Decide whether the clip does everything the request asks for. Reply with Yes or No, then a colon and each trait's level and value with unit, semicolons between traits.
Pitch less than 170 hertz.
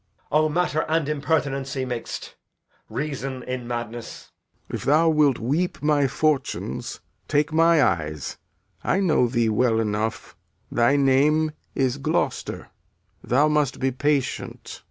Yes: medium, 140 Hz